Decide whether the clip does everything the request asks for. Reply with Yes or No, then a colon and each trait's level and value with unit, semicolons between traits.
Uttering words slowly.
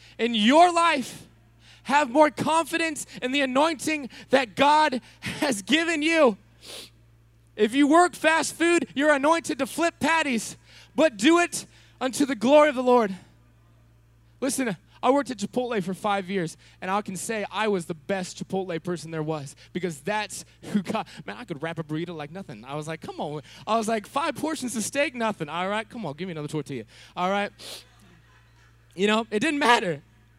No: average, 185 wpm